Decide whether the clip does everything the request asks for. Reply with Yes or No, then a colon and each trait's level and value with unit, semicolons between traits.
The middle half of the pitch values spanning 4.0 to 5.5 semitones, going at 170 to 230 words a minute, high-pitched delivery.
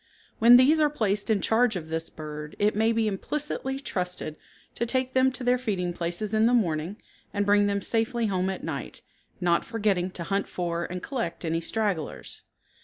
Yes: average, 4.9 semitones; average, 185 wpm; high, 205 Hz